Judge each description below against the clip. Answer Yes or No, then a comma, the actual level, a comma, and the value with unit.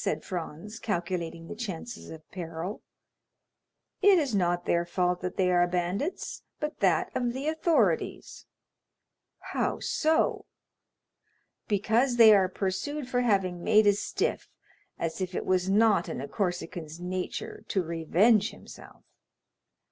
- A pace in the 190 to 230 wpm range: No, slow, 135 wpm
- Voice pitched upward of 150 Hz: Yes, high, 190 Hz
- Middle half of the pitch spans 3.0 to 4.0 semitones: No, average, 4.6 semitones